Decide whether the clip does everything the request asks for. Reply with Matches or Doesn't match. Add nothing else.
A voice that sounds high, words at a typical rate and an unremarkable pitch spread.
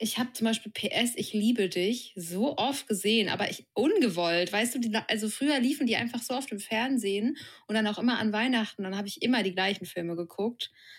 Doesn't match